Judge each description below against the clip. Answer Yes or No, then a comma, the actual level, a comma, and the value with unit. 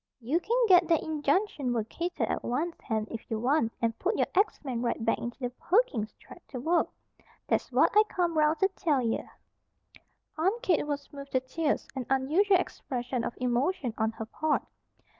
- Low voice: No, very high, 280 Hz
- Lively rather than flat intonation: Yes, wide, 6.1 semitones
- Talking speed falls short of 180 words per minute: No, average, 185 wpm